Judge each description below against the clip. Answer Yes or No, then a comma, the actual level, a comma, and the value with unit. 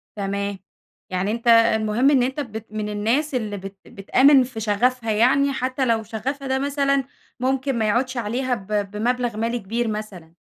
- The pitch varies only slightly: No, average, 3.7 semitones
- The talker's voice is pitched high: Yes, high, 230 Hz